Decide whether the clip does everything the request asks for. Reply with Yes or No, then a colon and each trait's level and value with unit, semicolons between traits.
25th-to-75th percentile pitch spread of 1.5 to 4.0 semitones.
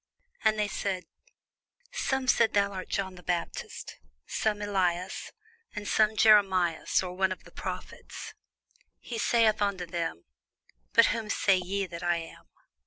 Yes: average, 2.9 semitones